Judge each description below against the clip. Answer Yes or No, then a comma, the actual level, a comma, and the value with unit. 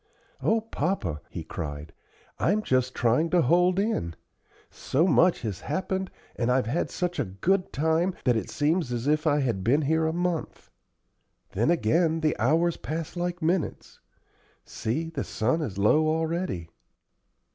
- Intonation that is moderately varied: No, wide, 6.2 semitones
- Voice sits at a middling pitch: Yes, medium, 155 Hz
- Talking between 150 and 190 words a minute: Yes, average, 155 wpm